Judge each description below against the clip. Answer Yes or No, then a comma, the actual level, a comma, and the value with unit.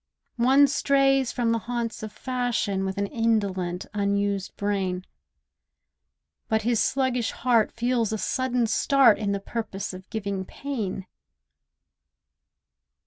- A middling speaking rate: No, slow, 120 wpm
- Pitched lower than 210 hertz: No, high, 220 Hz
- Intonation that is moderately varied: Yes, average, 3.7 semitones